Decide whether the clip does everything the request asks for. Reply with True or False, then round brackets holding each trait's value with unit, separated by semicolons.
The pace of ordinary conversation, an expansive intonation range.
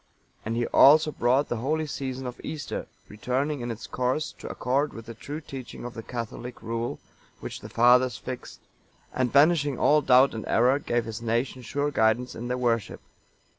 False (180 wpm; 3.1 semitones)